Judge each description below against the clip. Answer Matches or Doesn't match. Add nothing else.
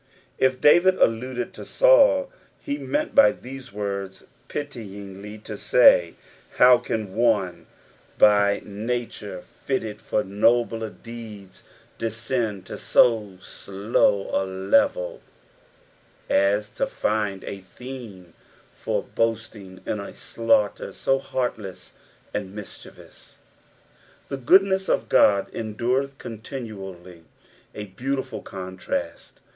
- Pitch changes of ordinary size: Matches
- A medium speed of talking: Doesn't match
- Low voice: Matches